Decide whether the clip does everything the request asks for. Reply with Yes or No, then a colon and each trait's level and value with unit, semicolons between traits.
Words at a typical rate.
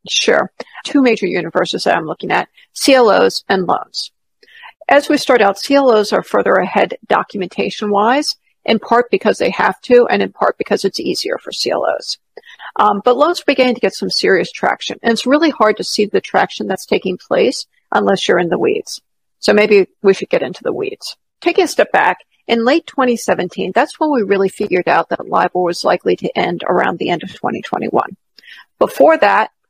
Yes: average, 190 wpm